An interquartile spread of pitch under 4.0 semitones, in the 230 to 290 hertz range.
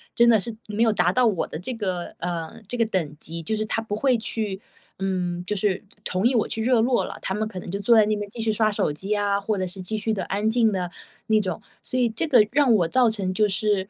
No: average, 3.1 semitones; high, 210 Hz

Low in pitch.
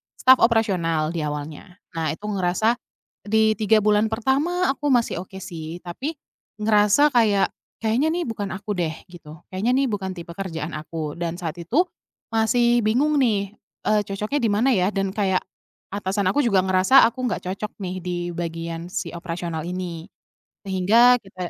No: high, 200 Hz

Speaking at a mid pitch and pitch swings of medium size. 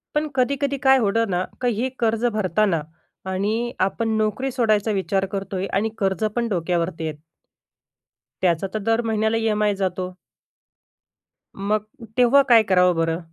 No: high, 210 Hz; average, 3.4 semitones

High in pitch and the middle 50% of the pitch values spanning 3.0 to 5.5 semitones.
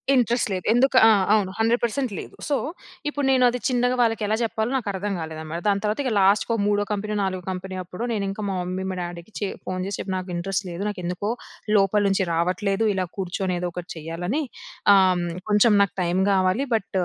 Yes: high, 195 Hz; average, 3.4 semitones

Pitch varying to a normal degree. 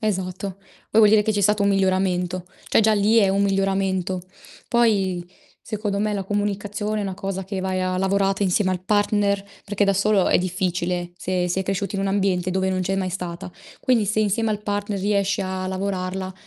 No: narrow, 1.7 semitones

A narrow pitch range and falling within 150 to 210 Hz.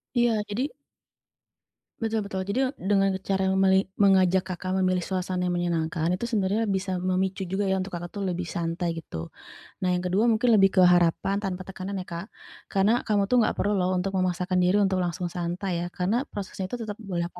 Yes: narrow, 2.0 semitones; high, 190 Hz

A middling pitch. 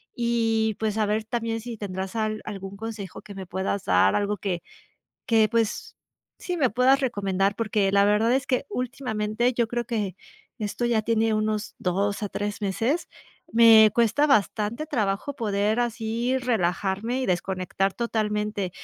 No: high, 215 Hz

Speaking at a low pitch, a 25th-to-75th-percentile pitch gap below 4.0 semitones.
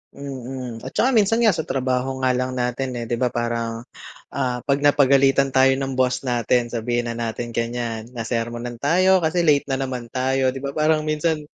Yes: low, 130 Hz; average, 2.7 semitones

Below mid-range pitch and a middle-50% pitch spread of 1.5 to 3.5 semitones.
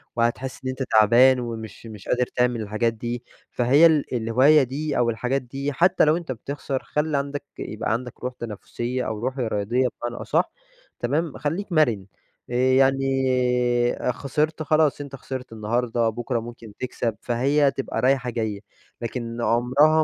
Yes: low, 125 Hz; average, 2.9 semitones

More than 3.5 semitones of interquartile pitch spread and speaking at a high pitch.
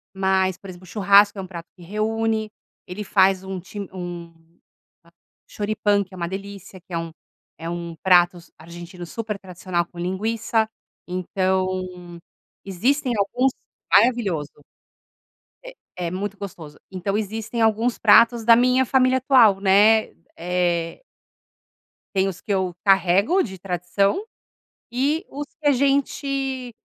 Yes: average, 3.9 semitones; high, 195 Hz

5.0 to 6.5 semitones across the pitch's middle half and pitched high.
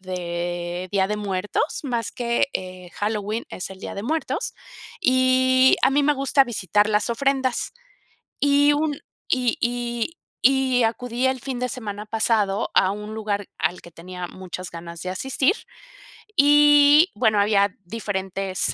Yes: wide, 5.4 semitones; high, 225 Hz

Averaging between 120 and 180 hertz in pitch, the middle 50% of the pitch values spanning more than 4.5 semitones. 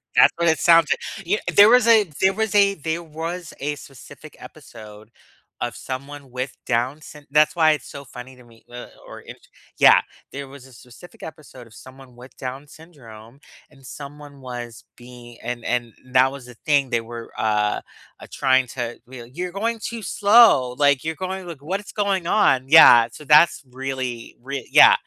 Yes: medium, 140 Hz; average, 5.2 semitones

